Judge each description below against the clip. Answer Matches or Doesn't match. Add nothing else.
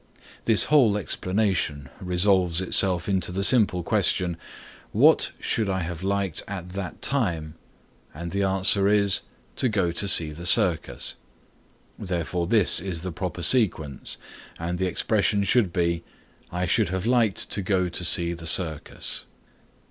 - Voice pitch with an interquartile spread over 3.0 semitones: Doesn't match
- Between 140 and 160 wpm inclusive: Matches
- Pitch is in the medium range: Doesn't match